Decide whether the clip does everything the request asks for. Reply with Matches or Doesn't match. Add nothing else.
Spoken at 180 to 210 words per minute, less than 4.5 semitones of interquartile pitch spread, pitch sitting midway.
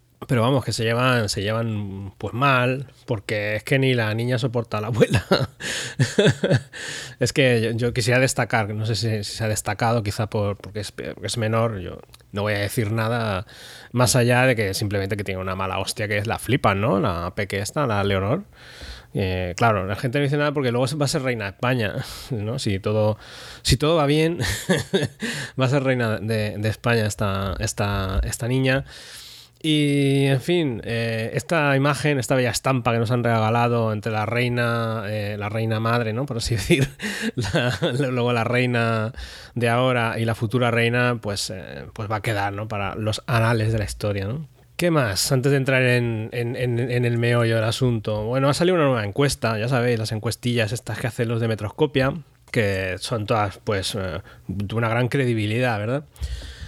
Doesn't match